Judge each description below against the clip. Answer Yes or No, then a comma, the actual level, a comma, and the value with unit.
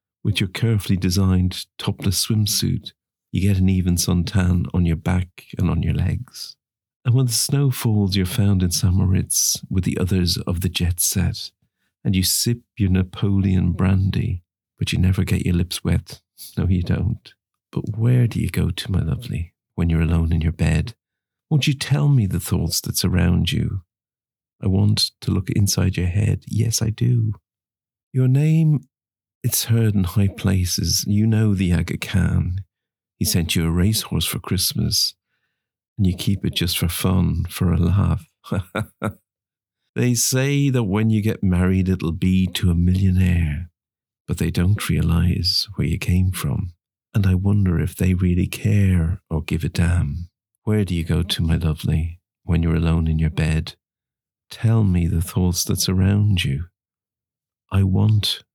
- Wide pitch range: No, average, 3.6 semitones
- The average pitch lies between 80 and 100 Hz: Yes, very low, 95 Hz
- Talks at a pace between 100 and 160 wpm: No, average, 170 wpm